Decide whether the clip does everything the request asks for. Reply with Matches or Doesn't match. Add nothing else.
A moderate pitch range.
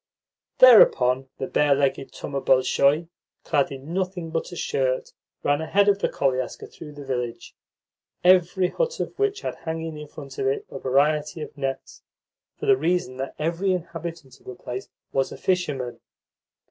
Matches